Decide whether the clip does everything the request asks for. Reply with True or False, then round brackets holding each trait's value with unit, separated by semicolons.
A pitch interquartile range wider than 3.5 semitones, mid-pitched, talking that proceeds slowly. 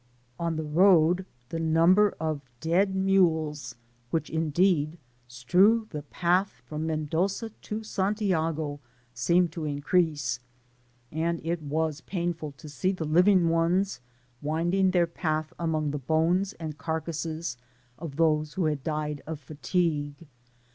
False (2.9 semitones; 160 Hz; 130 wpm)